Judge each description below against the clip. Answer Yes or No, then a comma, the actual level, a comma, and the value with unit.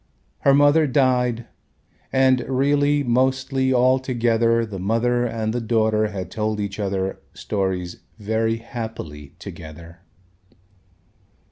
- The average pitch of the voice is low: Yes, low, 115 Hz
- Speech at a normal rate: No, slow, 105 wpm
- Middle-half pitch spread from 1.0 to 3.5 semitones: No, average, 3.9 semitones